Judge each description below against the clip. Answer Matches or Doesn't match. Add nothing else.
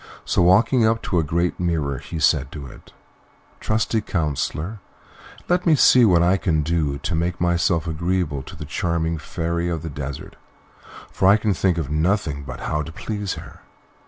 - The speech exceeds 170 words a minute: Matches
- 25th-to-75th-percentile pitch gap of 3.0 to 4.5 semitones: Matches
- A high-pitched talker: Doesn't match